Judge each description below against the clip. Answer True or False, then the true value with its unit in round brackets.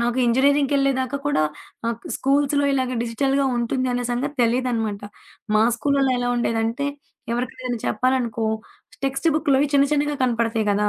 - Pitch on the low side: False (255 Hz)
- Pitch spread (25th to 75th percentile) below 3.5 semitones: True (2.9 semitones)